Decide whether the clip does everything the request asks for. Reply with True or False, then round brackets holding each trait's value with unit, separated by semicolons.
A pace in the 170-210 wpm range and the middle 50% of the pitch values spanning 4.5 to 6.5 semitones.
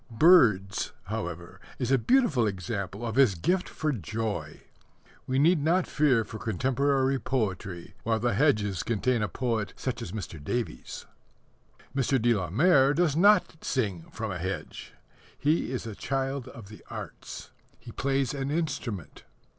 False (150 wpm; 5.3 semitones)